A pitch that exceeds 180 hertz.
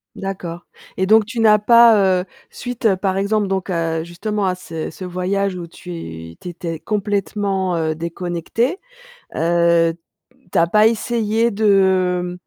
Yes: high, 190 Hz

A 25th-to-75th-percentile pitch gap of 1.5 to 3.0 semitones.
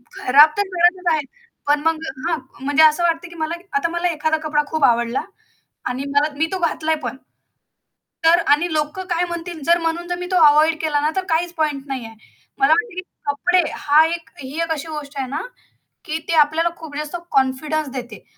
Yes: average, 2.7 semitones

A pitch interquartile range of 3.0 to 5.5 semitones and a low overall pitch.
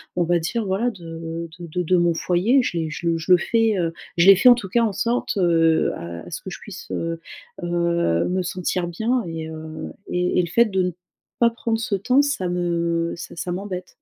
No: average, 4.1 semitones; medium, 180 Hz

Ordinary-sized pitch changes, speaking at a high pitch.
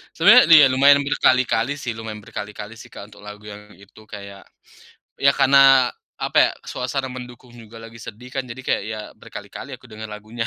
No: average, 3.7 semitones; low, 115 Hz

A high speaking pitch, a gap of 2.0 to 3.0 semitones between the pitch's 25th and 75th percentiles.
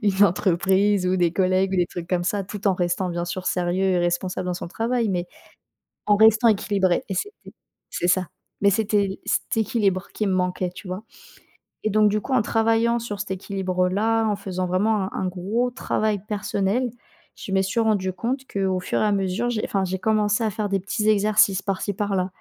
Yes: high, 195 Hz; narrow, 2.6 semitones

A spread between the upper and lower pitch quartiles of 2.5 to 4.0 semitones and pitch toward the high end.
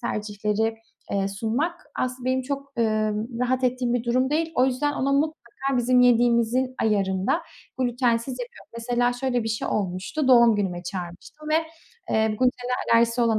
Yes: average, 2.8 semitones; high, 245 Hz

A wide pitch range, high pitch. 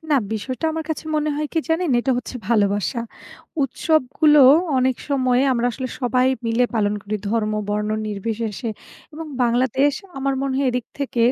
No: average, 3.8 semitones; very high, 250 Hz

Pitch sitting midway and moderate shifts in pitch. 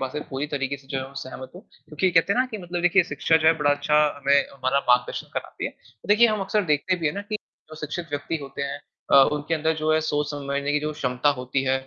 Yes: medium, 145 Hz; average, 3.2 semitones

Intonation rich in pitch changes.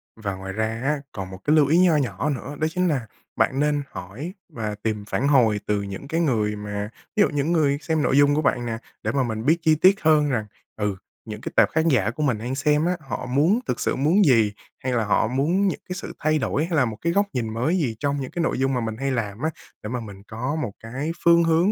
Yes: wide, 6.0 semitones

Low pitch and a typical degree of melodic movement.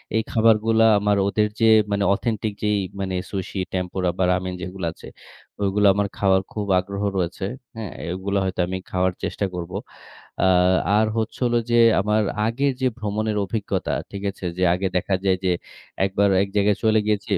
No: low, 100 Hz; narrow, 2.3 semitones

